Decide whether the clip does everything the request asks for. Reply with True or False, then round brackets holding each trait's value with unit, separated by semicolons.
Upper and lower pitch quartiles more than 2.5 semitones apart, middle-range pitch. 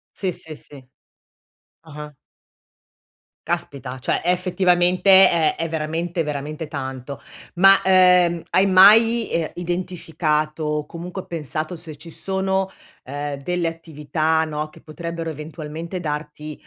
True (2.9 semitones; 165 Hz)